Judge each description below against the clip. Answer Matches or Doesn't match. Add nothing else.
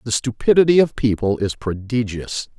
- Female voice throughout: Doesn't match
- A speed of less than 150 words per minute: Matches